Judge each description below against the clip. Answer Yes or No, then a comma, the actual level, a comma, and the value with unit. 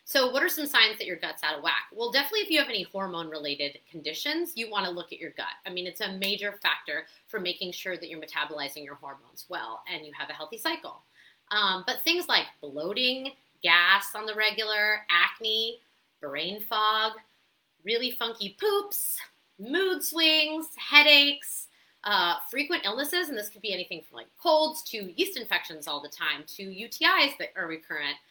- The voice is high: Yes, high, 215 Hz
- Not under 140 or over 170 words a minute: No, average, 185 wpm